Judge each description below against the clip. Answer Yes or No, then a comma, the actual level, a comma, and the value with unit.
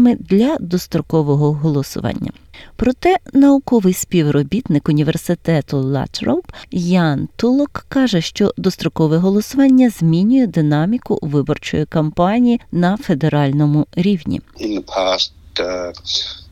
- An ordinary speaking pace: No, slow, 75 wpm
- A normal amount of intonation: No, wide, 7.3 semitones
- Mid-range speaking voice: Yes, medium, 175 Hz